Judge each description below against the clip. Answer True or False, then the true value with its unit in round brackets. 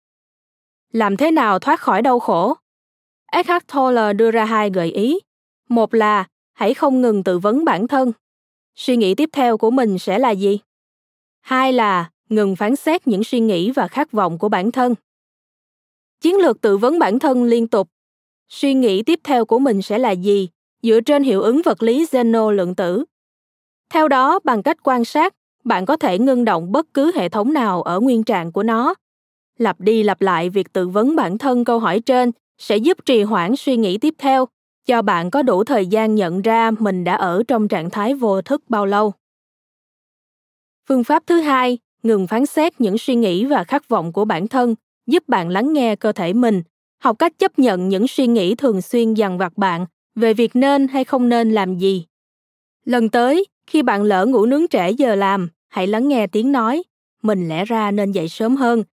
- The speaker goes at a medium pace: True (200 wpm)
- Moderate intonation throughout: True (4.5 semitones)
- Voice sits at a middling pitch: False (230 Hz)